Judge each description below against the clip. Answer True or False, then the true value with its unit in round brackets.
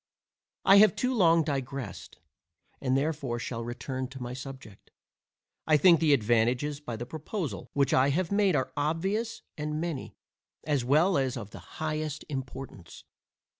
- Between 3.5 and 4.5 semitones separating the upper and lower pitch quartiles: True (4.0 semitones)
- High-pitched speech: False (140 Hz)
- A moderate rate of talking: True (150 wpm)